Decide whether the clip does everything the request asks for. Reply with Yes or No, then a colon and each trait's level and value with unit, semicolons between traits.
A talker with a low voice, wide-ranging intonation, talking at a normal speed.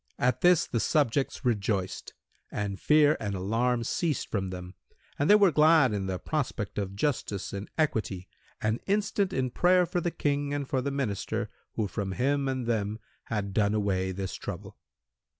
Yes: low, 115 Hz; wide, 6.3 semitones; average, 170 wpm